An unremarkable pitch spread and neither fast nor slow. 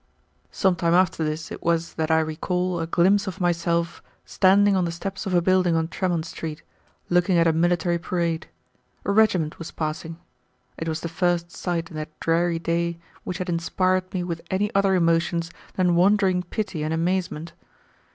No: narrow, 1.9 semitones; average, 180 wpm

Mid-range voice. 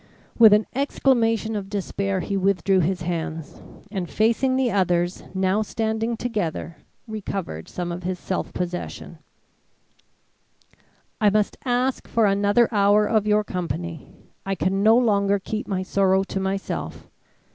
No: high, 200 Hz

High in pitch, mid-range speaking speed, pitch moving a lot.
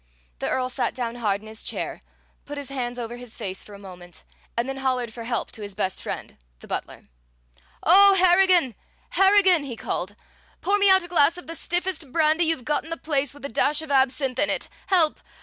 No: very high, 275 Hz; fast, 215 wpm; wide, 6.2 semitones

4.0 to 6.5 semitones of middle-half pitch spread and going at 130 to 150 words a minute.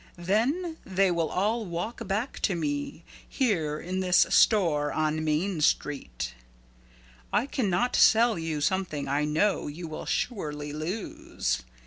Yes: wide, 5.5 semitones; slow, 135 wpm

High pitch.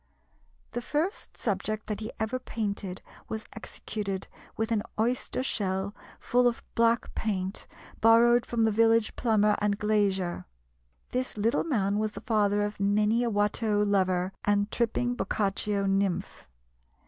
Yes: high, 210 Hz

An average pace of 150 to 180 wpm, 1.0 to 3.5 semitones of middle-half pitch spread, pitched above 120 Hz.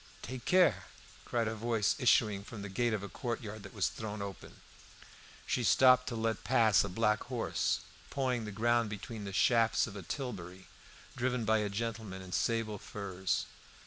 No: average, 175 wpm; average, 2.8 semitones; low, 110 Hz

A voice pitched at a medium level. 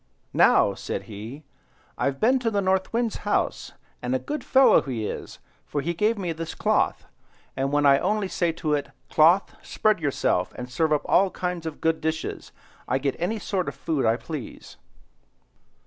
Yes: medium, 160 Hz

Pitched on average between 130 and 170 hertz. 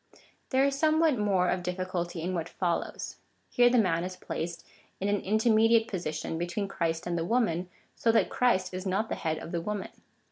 No: medium, 185 Hz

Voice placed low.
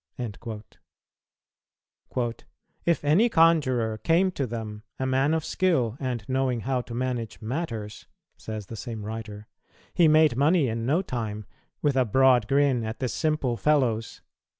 Yes: low, 125 Hz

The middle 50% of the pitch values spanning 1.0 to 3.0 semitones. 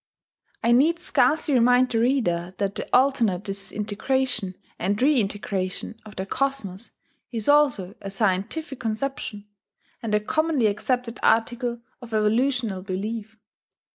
No: average, 4.4 semitones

